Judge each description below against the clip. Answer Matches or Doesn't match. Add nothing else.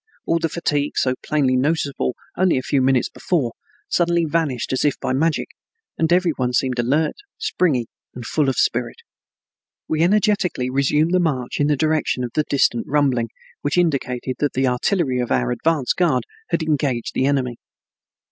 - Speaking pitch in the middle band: Matches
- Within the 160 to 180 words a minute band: Matches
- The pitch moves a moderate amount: Matches